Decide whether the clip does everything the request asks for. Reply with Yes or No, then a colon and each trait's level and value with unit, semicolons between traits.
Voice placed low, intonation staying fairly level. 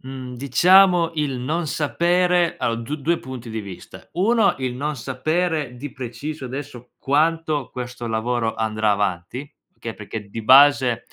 No: low, 130 Hz; average, 5.0 semitones